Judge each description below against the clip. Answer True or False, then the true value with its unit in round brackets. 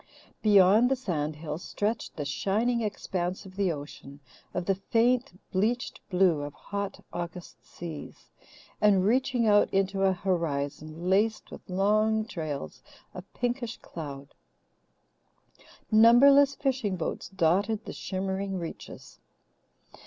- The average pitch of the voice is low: False (195 Hz)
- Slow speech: True (120 wpm)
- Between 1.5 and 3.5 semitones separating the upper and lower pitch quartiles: False (4.3 semitones)